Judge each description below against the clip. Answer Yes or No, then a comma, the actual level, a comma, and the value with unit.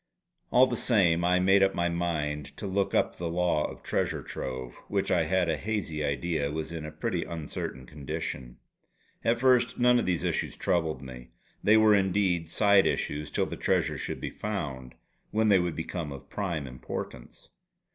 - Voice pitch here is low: Yes, very low, 85 Hz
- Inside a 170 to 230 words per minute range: Yes, average, 180 wpm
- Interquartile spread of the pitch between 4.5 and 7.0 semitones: Yes, average, 4.8 semitones